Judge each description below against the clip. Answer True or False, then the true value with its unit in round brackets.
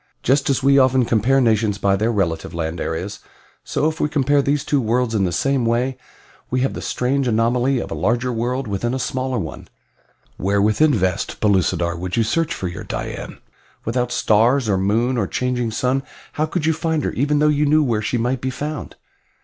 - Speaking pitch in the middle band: False (125 Hz)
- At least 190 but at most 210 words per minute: True (205 wpm)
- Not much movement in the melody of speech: False (4.5 semitones)